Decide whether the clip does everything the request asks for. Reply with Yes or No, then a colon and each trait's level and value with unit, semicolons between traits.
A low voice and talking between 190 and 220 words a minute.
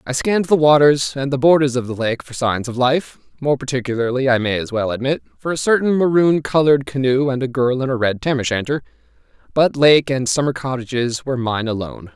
Yes: low, 130 Hz; fast, 205 wpm